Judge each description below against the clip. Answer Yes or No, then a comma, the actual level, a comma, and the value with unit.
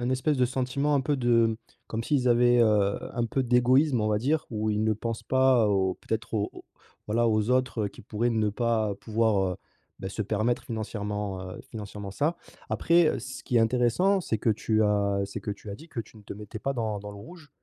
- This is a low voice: Yes, low, 115 Hz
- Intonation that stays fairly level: No, average, 3.3 semitones